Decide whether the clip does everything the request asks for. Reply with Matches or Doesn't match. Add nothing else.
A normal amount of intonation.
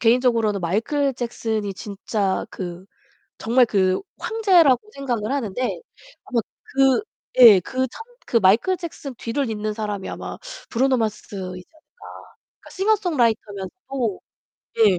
Matches